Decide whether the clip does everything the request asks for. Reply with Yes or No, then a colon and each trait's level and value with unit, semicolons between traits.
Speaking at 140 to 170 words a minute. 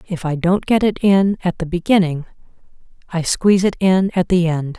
No: average, 200 wpm